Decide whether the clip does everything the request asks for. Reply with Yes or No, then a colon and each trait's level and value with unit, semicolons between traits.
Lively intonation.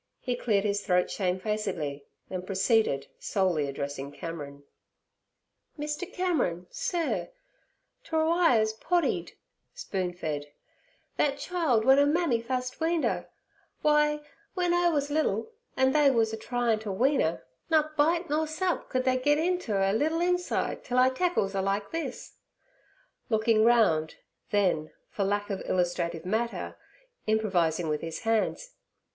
Yes: wide, 8.5 semitones